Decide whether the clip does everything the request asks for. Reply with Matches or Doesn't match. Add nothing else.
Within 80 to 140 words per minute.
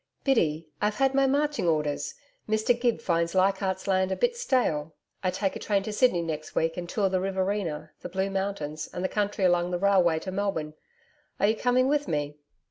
Doesn't match